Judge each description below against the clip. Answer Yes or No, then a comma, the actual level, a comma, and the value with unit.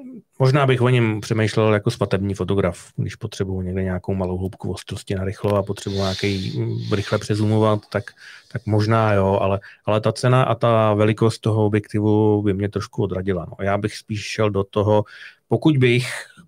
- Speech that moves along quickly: Yes, fast, 175 wpm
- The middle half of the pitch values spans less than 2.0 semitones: No, narrow, 2.5 semitones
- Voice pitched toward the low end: Yes, low, 105 Hz